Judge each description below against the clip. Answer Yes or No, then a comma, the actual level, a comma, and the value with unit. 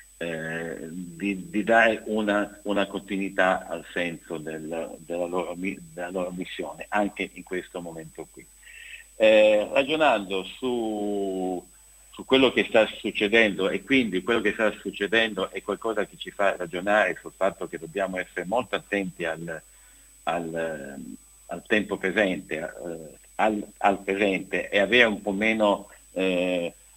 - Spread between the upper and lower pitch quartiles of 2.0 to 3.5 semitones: Yes, average, 2.8 semitones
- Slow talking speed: No, average, 140 wpm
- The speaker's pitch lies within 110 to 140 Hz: No, low, 100 Hz